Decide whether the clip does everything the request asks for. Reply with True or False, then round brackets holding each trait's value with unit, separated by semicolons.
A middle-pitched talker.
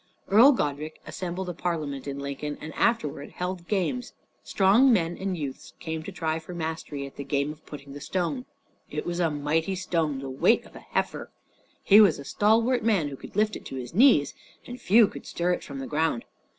True (165 Hz)